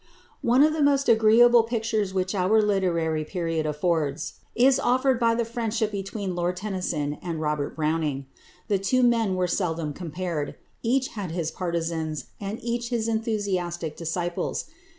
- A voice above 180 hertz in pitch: Yes, high, 190 Hz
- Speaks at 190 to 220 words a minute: No, average, 150 wpm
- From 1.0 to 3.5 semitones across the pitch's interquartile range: No, wide, 5.6 semitones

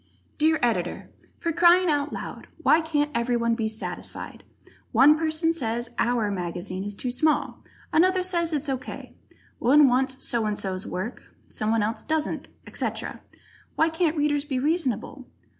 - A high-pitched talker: Yes, very high, 270 Hz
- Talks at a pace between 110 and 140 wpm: No, average, 155 wpm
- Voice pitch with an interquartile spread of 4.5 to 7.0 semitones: Yes, wide, 5.5 semitones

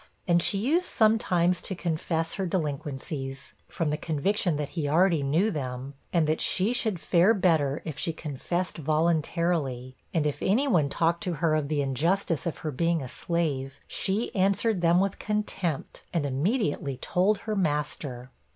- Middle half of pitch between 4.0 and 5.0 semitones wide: Yes, average, 4.3 semitones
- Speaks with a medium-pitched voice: Yes, medium, 165 Hz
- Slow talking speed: No, average, 165 wpm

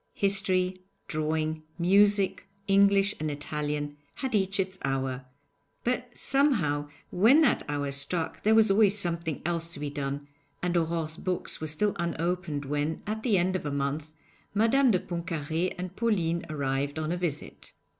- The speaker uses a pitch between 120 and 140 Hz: No, medium, 170 Hz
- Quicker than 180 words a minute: No, average, 155 wpm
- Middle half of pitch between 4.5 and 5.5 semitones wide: Yes, average, 4.9 semitones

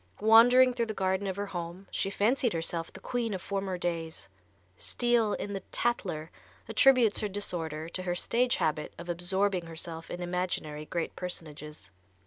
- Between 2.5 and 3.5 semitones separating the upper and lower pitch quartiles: No, average, 4.3 semitones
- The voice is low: No, medium, 185 Hz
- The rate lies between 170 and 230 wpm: No, average, 160 wpm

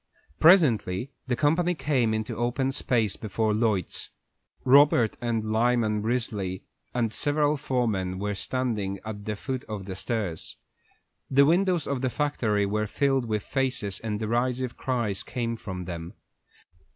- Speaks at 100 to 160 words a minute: Yes, average, 140 wpm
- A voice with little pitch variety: No, average, 4.0 semitones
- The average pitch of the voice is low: Yes, low, 115 Hz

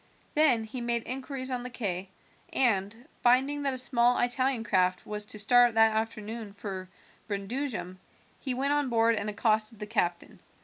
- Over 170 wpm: No, average, 165 wpm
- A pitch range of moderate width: Yes, average, 3.4 semitones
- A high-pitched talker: Yes, high, 230 Hz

